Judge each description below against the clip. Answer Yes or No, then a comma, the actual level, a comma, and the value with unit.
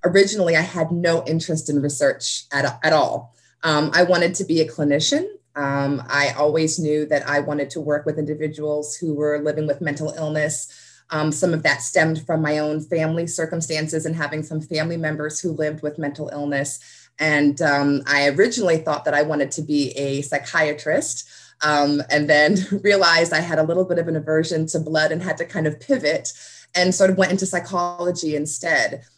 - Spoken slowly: No, average, 190 wpm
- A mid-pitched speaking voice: Yes, medium, 155 Hz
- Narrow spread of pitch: Yes, narrow, 2.2 semitones